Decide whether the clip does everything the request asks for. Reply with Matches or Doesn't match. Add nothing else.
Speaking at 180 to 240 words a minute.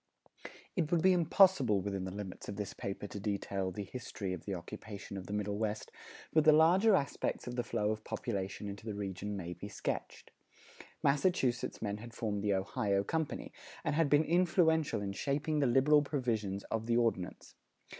Matches